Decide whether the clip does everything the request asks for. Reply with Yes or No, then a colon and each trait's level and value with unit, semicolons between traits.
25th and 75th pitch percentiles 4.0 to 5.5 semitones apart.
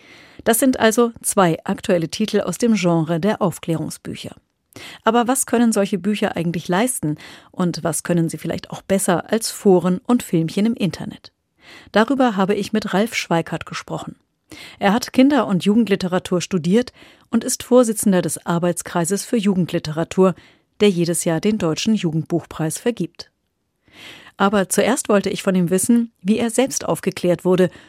Yes: average, 4.3 semitones